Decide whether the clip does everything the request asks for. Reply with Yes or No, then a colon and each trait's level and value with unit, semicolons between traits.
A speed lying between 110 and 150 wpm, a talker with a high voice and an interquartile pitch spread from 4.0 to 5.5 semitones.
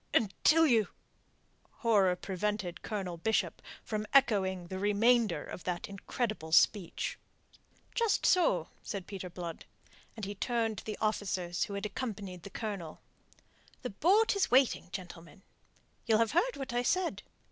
Yes: average, 140 wpm; high, 205 Hz; average, 4.4 semitones